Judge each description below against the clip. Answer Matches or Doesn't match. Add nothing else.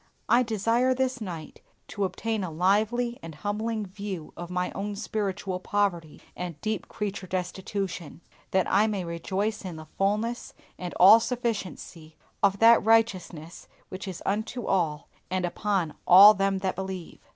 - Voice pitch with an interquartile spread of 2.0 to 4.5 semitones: Matches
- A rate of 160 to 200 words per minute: Doesn't match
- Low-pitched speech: Doesn't match